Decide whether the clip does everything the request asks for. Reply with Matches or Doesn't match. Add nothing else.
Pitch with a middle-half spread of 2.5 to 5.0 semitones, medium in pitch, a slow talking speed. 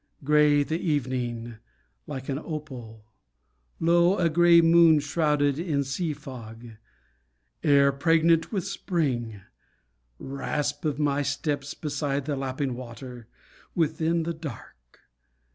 Matches